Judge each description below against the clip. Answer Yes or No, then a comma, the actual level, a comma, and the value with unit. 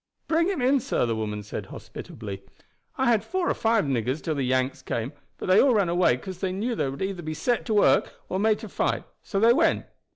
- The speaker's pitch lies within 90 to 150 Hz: No, high, 190 Hz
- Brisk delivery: Yes, fast, 235 wpm